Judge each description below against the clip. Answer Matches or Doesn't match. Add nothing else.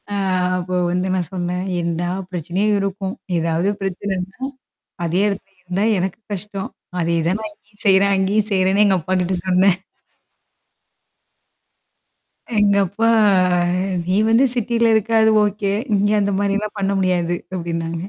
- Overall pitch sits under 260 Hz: Matches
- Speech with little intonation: Matches